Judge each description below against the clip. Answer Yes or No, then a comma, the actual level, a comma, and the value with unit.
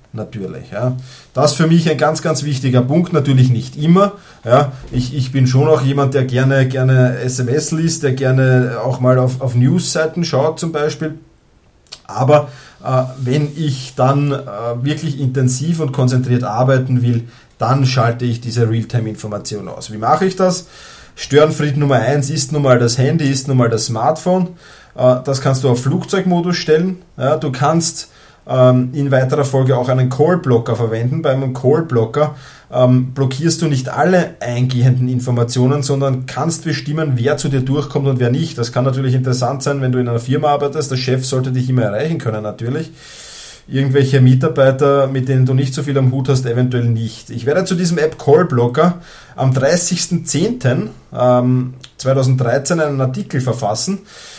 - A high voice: No, low, 135 Hz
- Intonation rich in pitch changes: No, average, 3.1 semitones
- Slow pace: No, average, 165 wpm